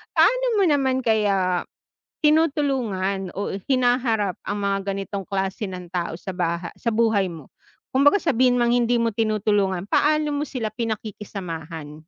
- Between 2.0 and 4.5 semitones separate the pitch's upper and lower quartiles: No, average, 5.0 semitones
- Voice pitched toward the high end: Yes, high, 215 Hz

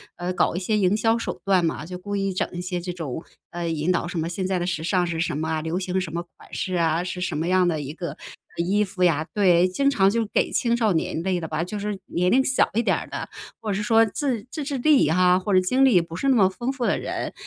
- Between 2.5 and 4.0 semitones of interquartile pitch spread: Yes, average, 3.5 semitones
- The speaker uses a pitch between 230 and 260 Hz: No, medium, 185 Hz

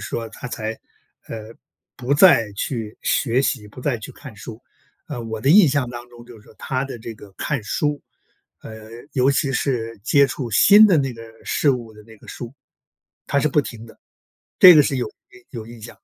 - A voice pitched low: Yes, low, 125 Hz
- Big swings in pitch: No, average, 3.6 semitones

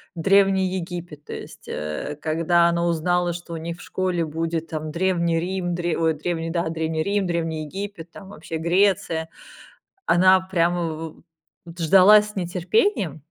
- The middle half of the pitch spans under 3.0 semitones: Yes, narrow, 2.4 semitones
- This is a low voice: No, medium, 170 Hz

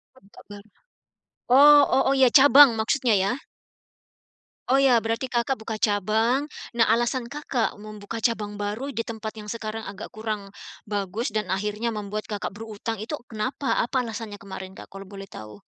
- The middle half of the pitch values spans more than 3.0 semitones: No, average, 2.7 semitones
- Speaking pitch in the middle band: No, high, 220 Hz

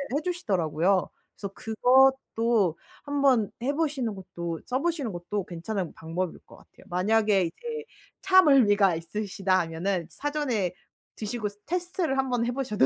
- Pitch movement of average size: No, wide, 6.7 semitones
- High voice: Yes, high, 215 Hz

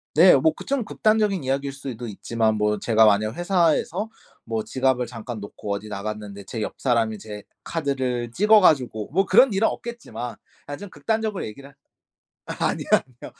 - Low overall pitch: Yes, low, 130 Hz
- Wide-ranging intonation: Yes, wide, 8.6 semitones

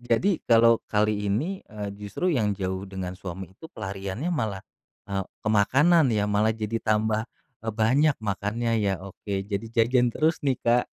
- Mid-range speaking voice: No, low, 110 Hz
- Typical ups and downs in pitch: Yes, average, 3.2 semitones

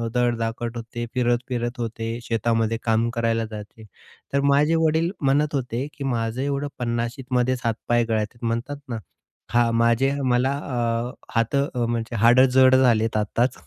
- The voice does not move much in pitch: Yes, narrow, 2.0 semitones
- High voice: No, low, 120 Hz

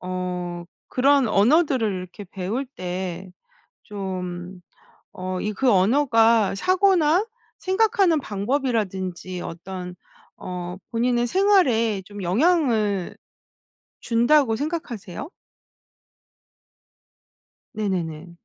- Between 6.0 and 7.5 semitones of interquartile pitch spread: Yes, wide, 6.9 semitones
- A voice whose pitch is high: Yes, high, 210 Hz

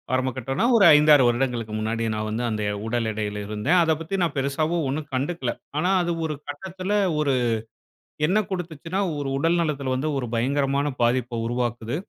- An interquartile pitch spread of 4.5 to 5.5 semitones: Yes, average, 5.1 semitones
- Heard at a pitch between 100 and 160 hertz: Yes, low, 135 Hz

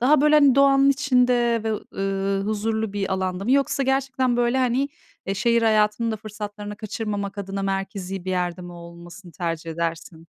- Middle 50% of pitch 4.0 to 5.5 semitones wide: Yes, average, 4.4 semitones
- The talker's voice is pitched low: No, high, 210 Hz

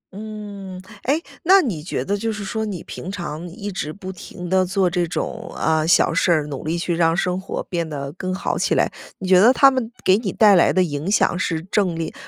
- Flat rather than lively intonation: No, average, 3.3 semitones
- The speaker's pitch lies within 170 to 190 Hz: Yes, medium, 185 Hz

